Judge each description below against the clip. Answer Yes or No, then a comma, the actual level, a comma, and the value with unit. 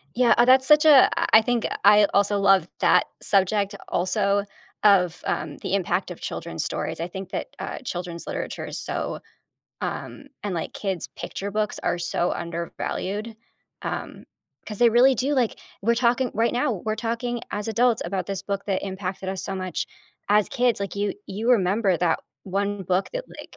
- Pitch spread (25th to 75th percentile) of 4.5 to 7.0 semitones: No, average, 3.8 semitones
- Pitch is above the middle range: Yes, high, 200 Hz